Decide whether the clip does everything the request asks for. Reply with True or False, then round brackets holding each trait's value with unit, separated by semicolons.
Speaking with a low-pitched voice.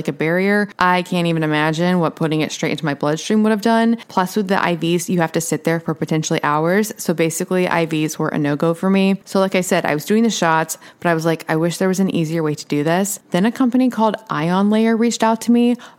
False (180 Hz)